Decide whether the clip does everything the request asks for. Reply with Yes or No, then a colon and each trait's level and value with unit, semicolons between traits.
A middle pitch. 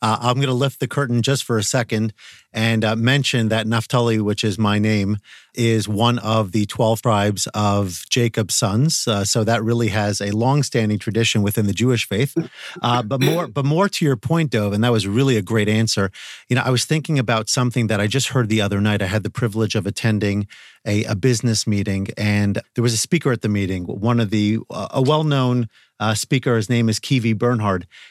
No: low, 115 Hz